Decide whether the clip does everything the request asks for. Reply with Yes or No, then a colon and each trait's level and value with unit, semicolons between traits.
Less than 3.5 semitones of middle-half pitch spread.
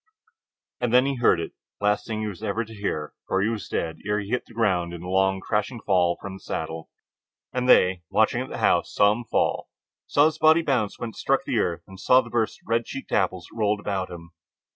No: average, 4.0 semitones